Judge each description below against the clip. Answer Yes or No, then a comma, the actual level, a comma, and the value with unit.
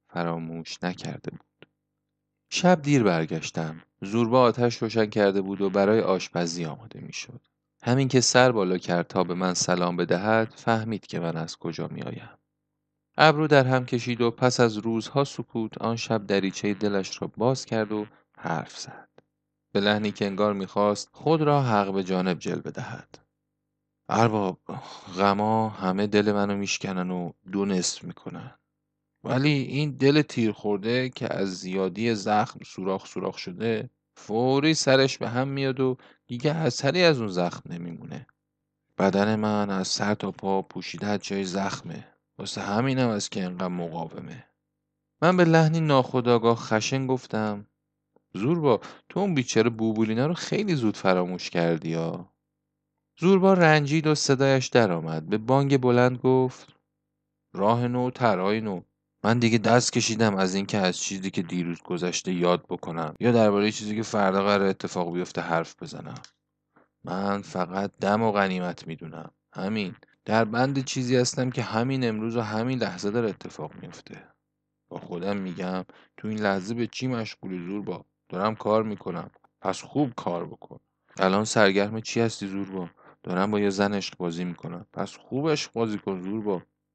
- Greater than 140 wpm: Yes, fast, 155 wpm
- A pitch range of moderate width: Yes, average, 4.9 semitones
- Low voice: Yes, low, 110 Hz